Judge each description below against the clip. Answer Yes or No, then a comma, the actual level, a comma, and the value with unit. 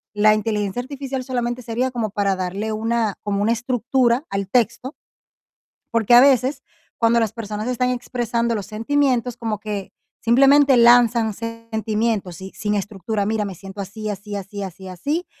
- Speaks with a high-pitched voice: Yes, high, 225 Hz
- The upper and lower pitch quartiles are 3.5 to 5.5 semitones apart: No, average, 3.0 semitones